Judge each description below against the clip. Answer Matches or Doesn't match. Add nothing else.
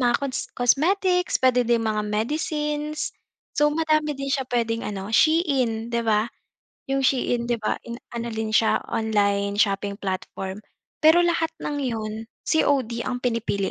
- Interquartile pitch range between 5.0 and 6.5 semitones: Matches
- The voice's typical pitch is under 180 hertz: Doesn't match